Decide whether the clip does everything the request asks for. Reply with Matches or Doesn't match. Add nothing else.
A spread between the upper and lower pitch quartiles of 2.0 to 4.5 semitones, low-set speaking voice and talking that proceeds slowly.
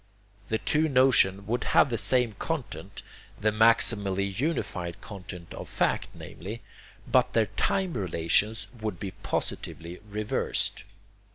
Matches